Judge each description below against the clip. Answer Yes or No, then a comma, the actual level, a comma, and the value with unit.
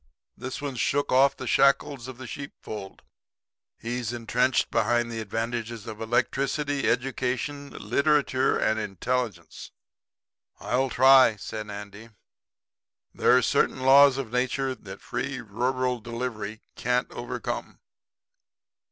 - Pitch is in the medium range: No, low, 125 Hz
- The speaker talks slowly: Yes, slow, 115 wpm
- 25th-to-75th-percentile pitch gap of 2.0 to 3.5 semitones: Yes, average, 2.8 semitones